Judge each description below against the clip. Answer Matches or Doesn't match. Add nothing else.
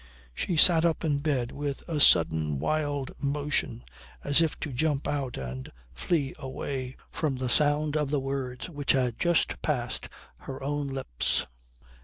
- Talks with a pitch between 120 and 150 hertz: Matches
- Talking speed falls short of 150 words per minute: Doesn't match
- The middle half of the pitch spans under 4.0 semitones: Matches